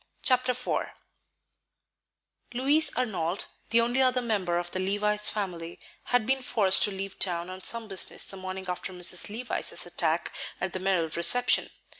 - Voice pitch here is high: Yes, high, 195 Hz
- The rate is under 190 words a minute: Yes, average, 155 wpm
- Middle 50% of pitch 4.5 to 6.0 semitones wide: Yes, average, 4.9 semitones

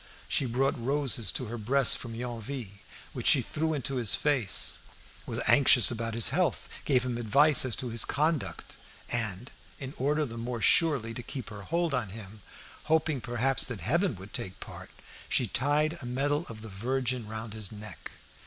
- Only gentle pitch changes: No, average, 3.9 semitones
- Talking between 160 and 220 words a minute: Yes, average, 180 wpm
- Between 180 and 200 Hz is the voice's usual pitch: No, low, 125 Hz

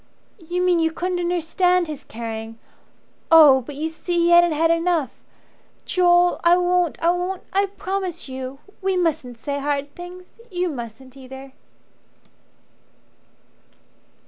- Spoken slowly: Yes, slow, 130 wpm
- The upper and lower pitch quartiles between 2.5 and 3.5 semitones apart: No, average, 4.4 semitones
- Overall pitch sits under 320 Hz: No, very high, 335 Hz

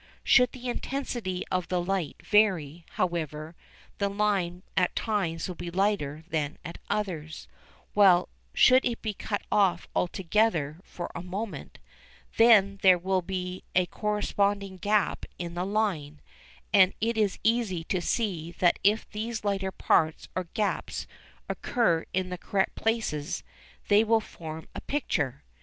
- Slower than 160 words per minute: Yes, average, 145 wpm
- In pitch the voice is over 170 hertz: Yes, high, 190 Hz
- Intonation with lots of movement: No, average, 3.5 semitones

